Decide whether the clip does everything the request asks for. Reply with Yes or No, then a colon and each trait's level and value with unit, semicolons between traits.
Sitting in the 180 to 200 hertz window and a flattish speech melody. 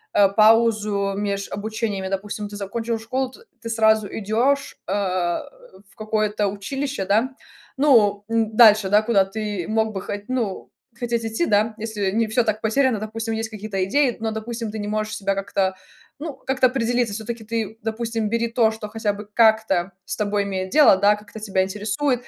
No: high, 215 Hz; narrow, 2.1 semitones